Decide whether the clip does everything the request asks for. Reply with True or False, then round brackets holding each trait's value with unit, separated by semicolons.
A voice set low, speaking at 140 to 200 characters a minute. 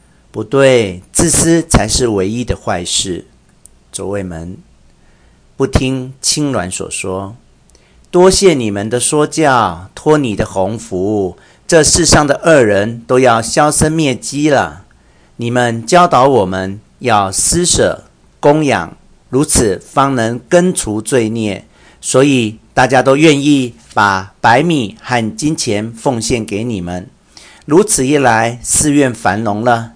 True (115 Hz; 180 characters per minute)